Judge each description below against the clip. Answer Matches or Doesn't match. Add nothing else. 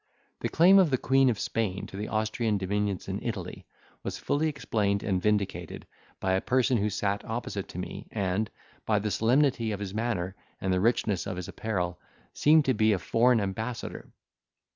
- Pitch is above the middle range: Doesn't match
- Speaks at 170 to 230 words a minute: Matches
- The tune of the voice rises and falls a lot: Doesn't match